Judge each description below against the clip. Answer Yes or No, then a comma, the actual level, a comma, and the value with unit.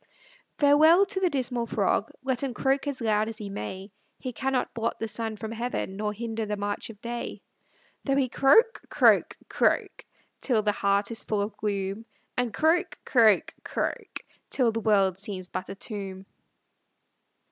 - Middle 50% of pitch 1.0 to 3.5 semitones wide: No, average, 4.2 semitones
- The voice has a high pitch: Yes, high, 225 Hz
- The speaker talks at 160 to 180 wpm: Yes, average, 170 wpm